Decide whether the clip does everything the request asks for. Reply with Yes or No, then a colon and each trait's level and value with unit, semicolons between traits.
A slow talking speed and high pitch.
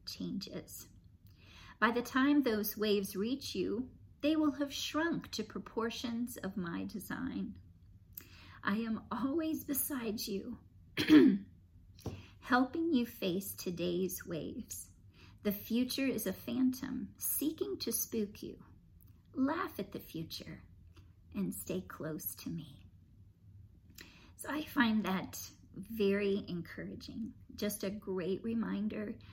Yes: slow, 115 wpm; high, 200 Hz